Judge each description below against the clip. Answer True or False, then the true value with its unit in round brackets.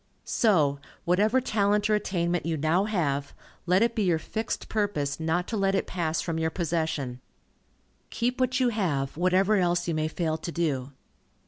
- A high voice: False (175 Hz)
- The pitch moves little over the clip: False (4.6 semitones)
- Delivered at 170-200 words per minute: True (175 wpm)